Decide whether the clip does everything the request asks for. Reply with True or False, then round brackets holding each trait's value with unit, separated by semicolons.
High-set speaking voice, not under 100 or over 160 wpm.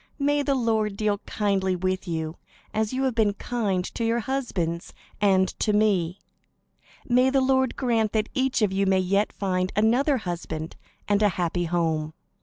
False (205 Hz; 170 wpm)